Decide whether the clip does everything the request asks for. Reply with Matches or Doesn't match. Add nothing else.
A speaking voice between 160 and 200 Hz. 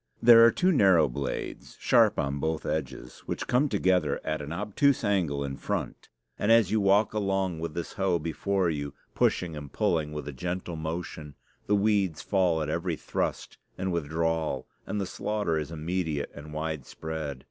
Doesn't match